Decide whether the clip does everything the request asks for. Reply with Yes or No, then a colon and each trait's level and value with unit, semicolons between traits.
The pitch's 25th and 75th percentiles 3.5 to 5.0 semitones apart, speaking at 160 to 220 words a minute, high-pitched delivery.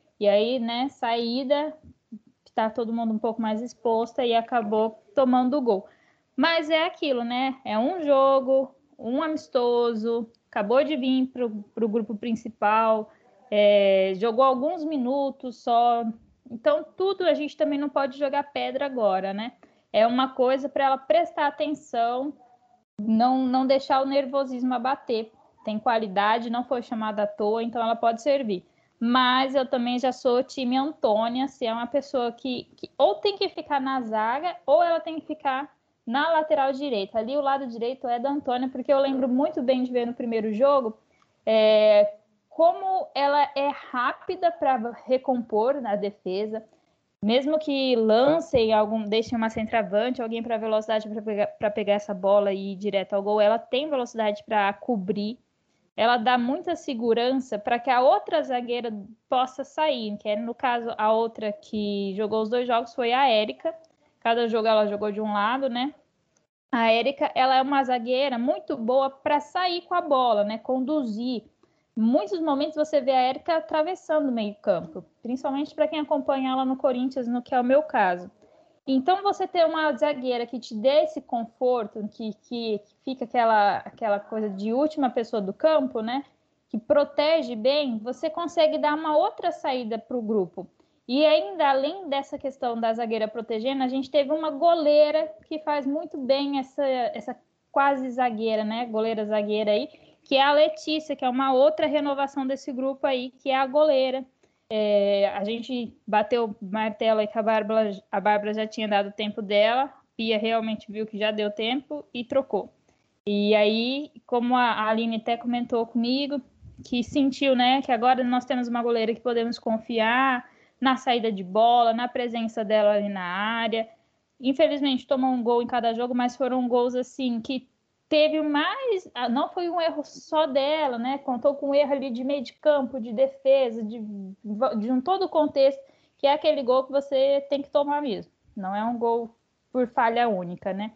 Yes: average, 4.1 semitones; average, 175 wpm; very high, 255 Hz